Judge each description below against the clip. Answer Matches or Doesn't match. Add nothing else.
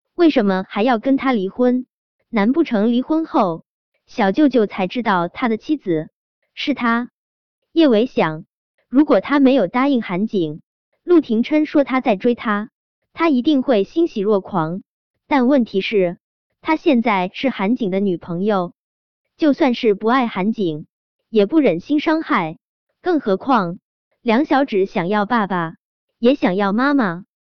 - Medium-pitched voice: Doesn't match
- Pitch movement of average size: Doesn't match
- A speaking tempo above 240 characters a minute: Doesn't match